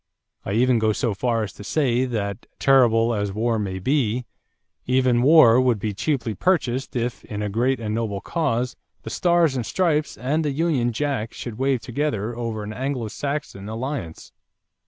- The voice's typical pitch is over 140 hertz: No, low, 120 Hz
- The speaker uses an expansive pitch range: No, average, 3.8 semitones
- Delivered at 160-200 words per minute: Yes, average, 175 wpm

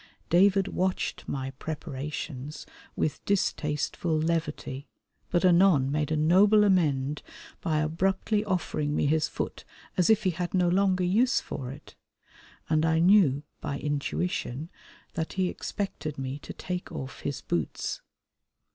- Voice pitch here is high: No, medium, 160 Hz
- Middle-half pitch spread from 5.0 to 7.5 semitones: No, average, 4.1 semitones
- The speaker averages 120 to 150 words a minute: Yes, slow, 135 wpm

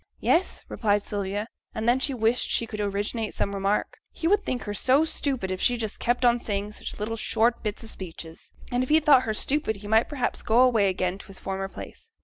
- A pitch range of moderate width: Yes, average, 3.7 semitones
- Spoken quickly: Yes, fast, 225 wpm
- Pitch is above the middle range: Yes, high, 220 Hz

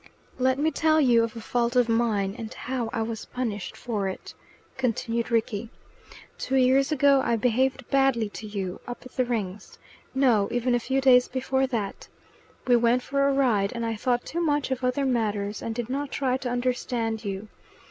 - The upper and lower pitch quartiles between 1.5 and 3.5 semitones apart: Yes, average, 2.8 semitones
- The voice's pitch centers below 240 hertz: No, high, 245 Hz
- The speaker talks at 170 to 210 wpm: Yes, average, 190 wpm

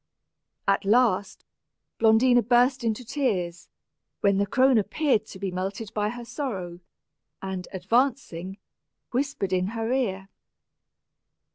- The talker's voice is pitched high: Yes, high, 215 Hz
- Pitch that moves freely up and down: No, average, 4.5 semitones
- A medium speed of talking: No, slow, 115 wpm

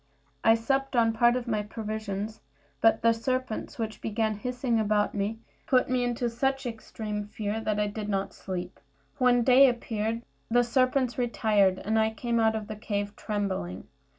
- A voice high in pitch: Yes, high, 225 Hz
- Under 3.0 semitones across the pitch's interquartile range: Yes, narrow, 2.5 semitones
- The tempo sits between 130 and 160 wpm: No, average, 170 wpm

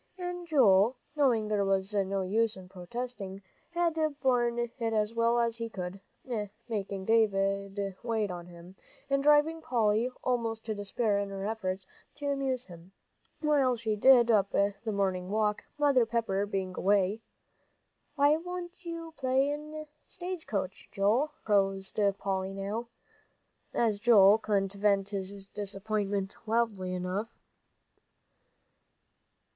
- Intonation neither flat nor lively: Yes, average, 4.2 semitones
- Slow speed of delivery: Yes, slow, 130 wpm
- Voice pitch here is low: No, high, 215 Hz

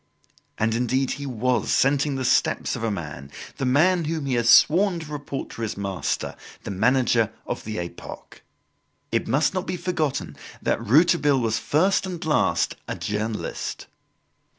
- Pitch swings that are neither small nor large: No, wide, 5.7 semitones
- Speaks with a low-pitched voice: Yes, low, 130 Hz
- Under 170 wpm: Yes, average, 160 wpm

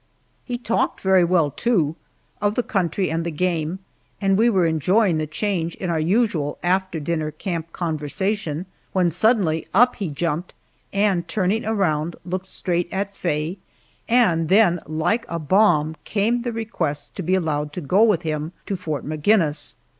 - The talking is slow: No, average, 160 wpm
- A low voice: No, medium, 175 Hz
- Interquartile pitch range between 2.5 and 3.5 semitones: No, average, 4.3 semitones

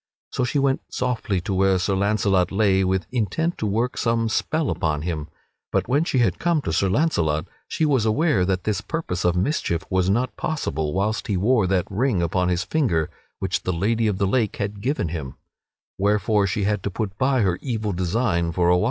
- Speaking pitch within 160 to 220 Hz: No, low, 100 Hz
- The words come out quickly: Yes, fast, 210 wpm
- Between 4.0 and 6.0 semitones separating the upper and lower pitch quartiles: Yes, average, 5.0 semitones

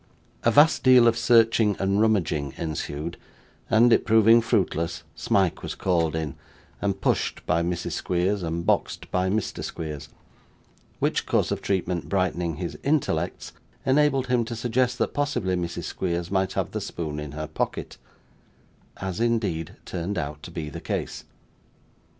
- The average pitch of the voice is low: Yes, very low, 95 Hz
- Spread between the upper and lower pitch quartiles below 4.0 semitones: No, wide, 5.4 semitones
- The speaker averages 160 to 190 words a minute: No, average, 150 wpm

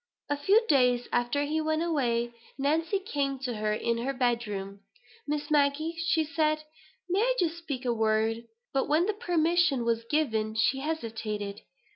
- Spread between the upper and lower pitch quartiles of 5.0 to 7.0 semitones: Yes, average, 5.3 semitones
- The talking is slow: No, average, 165 wpm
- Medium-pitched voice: No, very high, 280 Hz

